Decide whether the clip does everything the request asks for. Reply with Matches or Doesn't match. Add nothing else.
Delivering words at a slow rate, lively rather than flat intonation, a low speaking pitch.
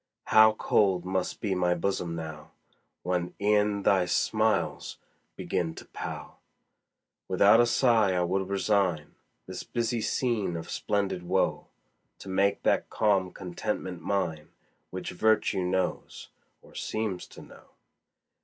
Doesn't match